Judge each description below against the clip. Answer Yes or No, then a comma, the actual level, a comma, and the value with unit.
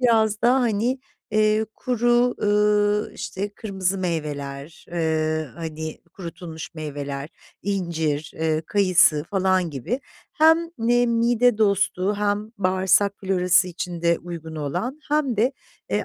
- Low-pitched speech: No, high, 190 Hz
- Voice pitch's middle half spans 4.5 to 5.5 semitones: Yes, average, 5.2 semitones